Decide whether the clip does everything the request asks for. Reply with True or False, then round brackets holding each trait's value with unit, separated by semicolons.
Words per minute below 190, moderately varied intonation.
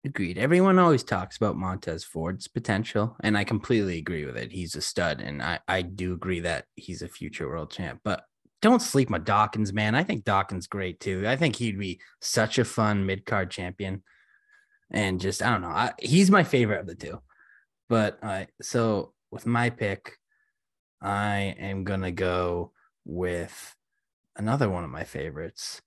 True (180 wpm; 4.5 semitones)